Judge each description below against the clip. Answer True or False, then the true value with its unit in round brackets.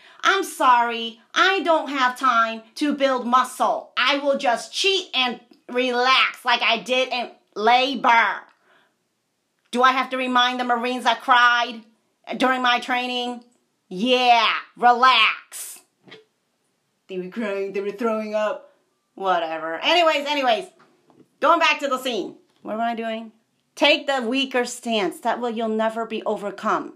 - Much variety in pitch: False (3.4 semitones)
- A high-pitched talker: True (245 Hz)